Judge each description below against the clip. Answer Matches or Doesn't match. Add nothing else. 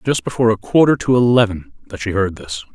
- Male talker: Matches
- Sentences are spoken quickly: Matches